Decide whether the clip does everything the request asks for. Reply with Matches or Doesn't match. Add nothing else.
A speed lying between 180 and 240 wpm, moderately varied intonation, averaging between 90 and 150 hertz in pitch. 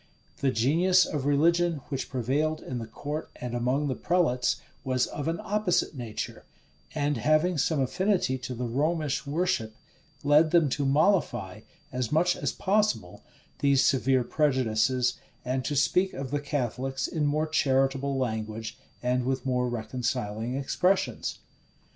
Doesn't match